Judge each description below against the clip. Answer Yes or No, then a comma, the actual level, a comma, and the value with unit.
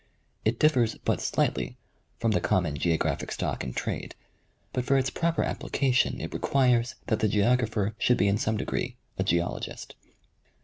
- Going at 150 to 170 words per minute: Yes, average, 160 wpm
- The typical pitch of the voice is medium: No, low, 115 Hz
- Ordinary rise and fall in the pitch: Yes, average, 4.0 semitones